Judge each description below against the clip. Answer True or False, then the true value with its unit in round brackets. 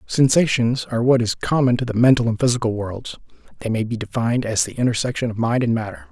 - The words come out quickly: True (215 wpm)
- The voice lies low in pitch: True (120 Hz)